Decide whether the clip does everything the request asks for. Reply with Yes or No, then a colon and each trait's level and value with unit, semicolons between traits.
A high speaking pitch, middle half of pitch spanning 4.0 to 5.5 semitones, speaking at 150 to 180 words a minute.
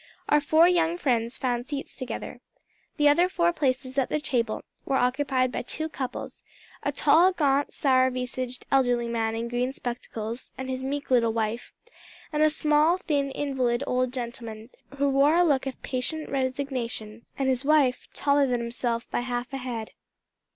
No: very high, 260 Hz; average, 3.0 semitones; average, 170 wpm